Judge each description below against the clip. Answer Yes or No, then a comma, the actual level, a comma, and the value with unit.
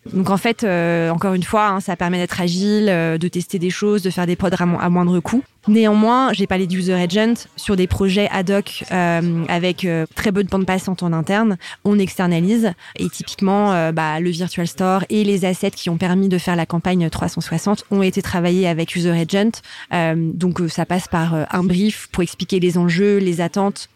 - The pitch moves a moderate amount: No, narrow, 2.3 semitones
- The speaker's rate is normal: Yes, average, 210 wpm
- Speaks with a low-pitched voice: No, medium, 185 Hz